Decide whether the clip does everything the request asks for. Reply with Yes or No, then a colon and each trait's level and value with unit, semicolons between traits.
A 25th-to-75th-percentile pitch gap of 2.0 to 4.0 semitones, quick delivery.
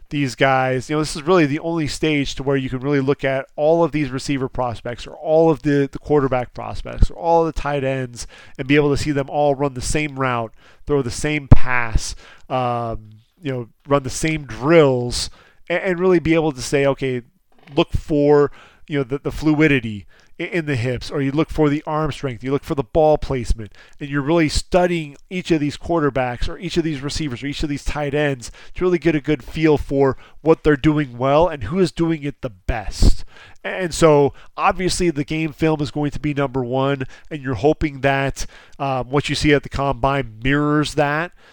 Yes: average, 2.9 semitones; fast, 215 wpm